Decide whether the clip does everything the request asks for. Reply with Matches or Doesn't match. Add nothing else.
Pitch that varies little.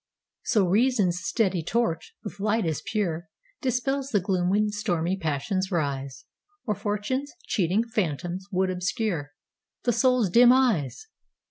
Doesn't match